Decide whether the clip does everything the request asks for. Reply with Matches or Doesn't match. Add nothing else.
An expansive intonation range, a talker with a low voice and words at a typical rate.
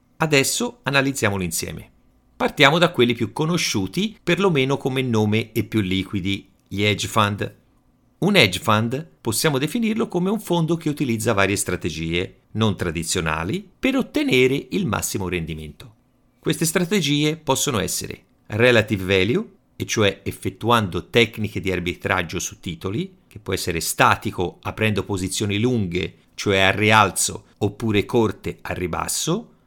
Matches